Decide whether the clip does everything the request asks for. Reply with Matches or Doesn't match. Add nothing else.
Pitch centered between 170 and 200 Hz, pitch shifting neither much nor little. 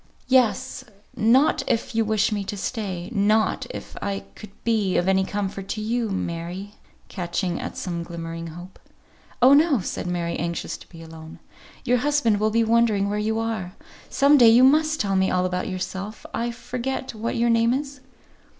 Doesn't match